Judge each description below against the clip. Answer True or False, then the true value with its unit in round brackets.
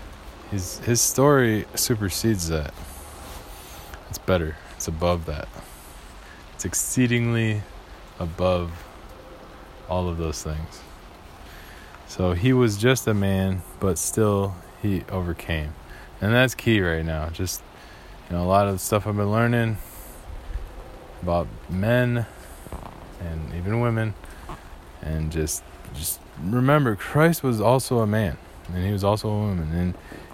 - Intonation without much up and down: False (5.0 semitones)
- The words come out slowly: True (125 wpm)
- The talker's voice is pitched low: True (90 Hz)